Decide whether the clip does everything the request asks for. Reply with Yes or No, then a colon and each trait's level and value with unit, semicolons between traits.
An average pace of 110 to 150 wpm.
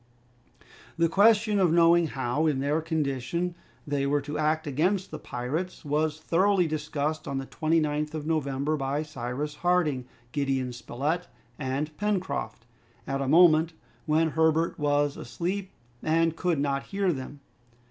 Yes: average, 140 wpm